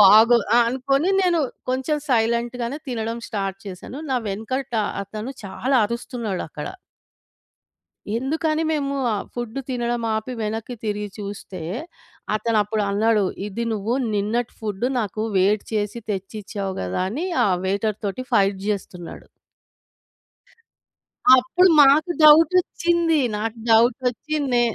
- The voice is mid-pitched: No, high, 230 Hz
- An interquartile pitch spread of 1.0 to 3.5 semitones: No, average, 4.0 semitones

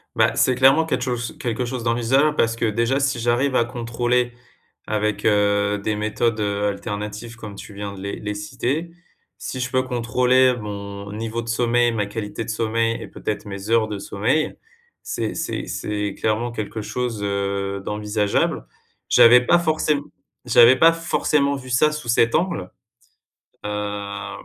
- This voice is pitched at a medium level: No, low, 115 Hz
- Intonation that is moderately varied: Yes, average, 3.3 semitones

